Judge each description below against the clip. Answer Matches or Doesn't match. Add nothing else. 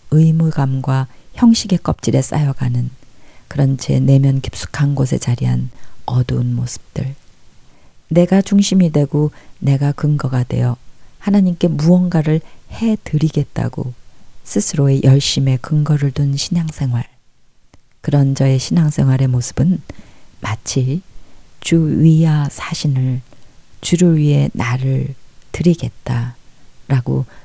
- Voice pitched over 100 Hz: Matches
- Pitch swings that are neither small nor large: Matches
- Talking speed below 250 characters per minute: Matches